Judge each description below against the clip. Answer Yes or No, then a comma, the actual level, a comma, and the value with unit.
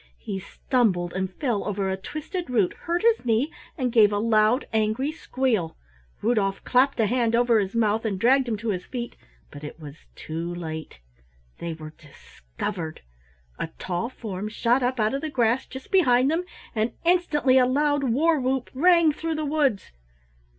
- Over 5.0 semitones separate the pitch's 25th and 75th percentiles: Yes, wide, 5.5 semitones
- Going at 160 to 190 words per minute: Yes, average, 175 wpm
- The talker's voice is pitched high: Yes, high, 235 Hz